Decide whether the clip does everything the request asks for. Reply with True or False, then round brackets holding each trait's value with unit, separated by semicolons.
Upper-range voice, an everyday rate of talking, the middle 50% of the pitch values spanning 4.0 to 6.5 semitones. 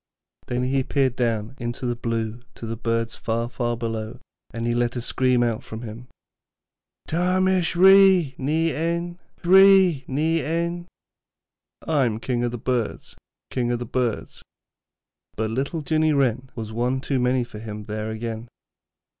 False (125 Hz; 160 wpm; 5.4 semitones)